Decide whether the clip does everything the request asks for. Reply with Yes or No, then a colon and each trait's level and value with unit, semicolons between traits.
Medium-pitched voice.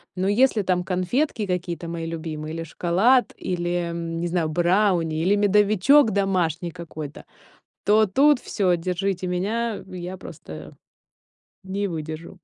Yes: medium, 180 Hz